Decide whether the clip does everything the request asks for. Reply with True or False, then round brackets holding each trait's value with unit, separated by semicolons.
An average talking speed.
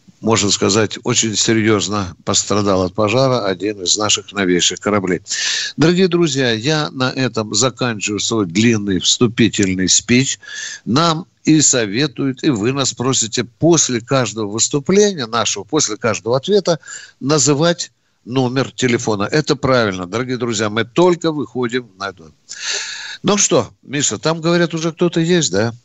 True (130 wpm)